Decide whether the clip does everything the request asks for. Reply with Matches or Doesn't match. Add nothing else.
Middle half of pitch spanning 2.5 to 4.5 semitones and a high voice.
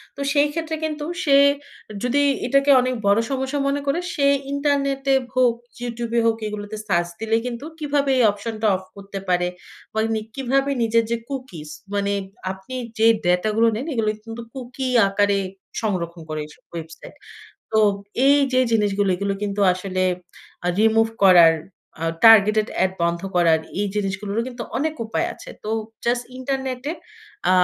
Doesn't match